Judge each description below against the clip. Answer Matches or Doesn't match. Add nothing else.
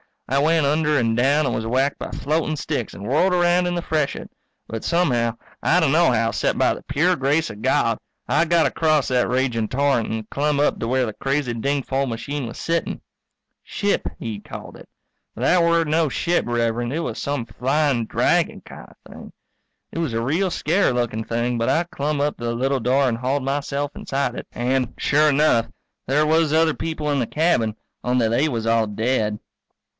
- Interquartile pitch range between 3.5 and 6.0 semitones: Matches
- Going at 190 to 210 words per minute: Matches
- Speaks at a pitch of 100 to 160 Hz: Matches